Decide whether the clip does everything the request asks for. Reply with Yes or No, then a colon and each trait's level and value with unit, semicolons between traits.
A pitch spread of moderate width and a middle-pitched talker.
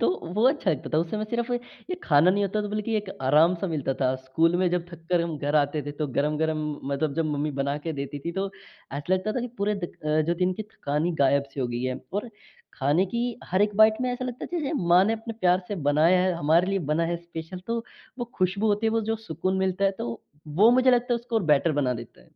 No: wide, 5.8 semitones; medium, 175 Hz